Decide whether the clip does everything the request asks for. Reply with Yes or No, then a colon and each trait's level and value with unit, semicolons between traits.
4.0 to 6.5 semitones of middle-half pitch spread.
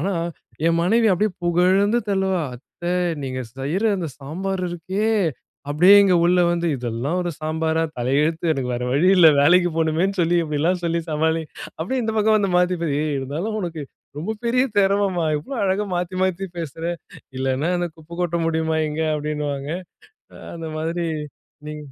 No: average, 3.6 semitones